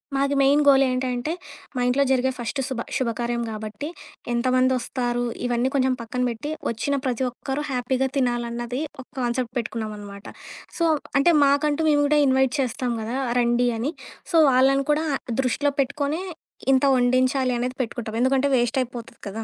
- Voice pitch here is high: Yes, very high, 255 Hz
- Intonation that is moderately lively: No, narrow, 2.3 semitones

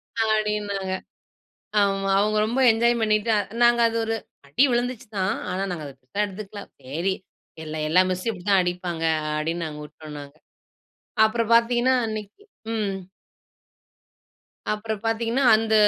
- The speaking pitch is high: Yes, high, 210 Hz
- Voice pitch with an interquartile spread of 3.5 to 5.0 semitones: Yes, average, 4.0 semitones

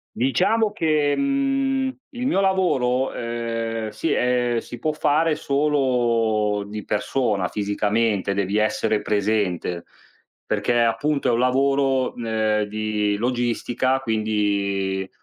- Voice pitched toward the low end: Yes, low, 115 Hz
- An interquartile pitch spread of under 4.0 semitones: No, average, 4.8 semitones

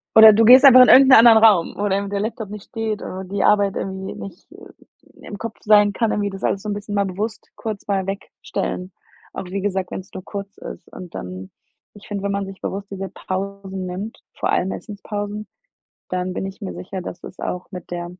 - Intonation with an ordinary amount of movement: No, narrow, 1.8 semitones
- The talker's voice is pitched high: Yes, high, 200 Hz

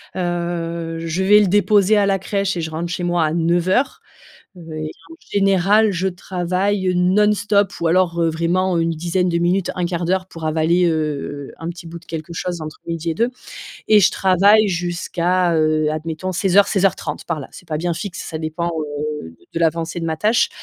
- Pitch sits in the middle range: Yes, medium, 175 Hz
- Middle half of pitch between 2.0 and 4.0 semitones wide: Yes, narrow, 2.4 semitones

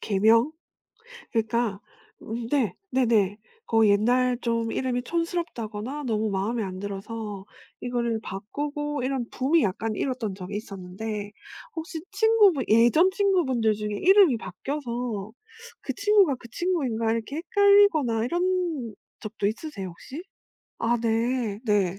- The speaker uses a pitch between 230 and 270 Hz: Yes, high, 235 Hz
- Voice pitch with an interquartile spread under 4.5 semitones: No, wide, 5.5 semitones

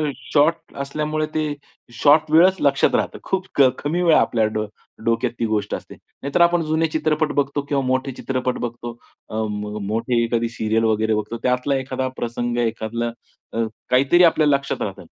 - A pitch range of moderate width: Yes, average, 4.7 semitones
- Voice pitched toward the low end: Yes, low, 130 Hz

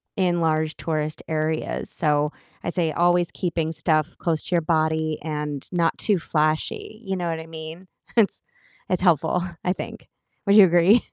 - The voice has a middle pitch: Yes, medium, 165 Hz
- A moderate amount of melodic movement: No, narrow, 2.2 semitones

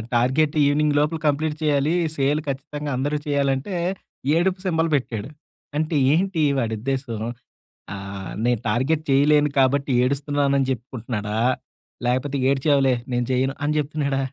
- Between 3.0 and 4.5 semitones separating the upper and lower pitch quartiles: No, narrow, 2.6 semitones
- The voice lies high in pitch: No, medium, 140 Hz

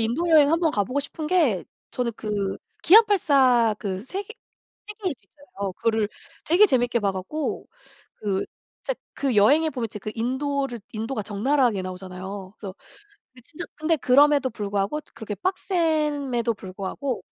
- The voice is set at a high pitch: Yes, very high, 250 Hz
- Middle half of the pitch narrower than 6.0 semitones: No, wide, 6.6 semitones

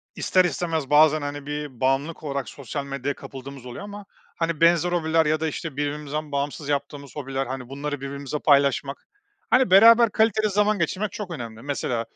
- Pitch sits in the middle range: Yes, medium, 145 Hz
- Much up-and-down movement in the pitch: No, average, 3.3 semitones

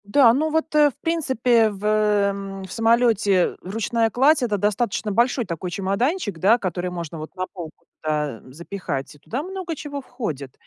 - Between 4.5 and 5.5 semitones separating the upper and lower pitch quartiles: Yes, average, 5.2 semitones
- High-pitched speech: Yes, high, 210 Hz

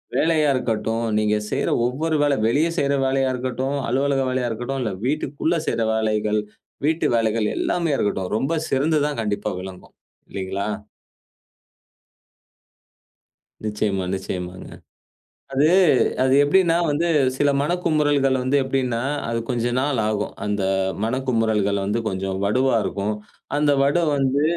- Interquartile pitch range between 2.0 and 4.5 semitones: No, average, 5.0 semitones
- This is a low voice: Yes, low, 130 Hz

